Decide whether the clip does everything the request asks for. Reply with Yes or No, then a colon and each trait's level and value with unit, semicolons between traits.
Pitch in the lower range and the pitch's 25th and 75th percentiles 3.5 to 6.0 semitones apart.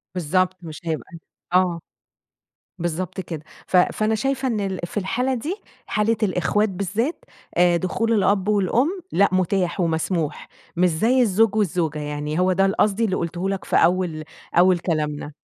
No: medium, 185 Hz; average, 3.8 semitones